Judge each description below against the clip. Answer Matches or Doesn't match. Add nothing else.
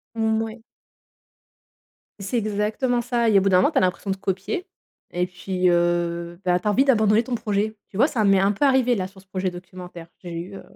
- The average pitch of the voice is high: Matches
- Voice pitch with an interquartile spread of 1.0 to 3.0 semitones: Doesn't match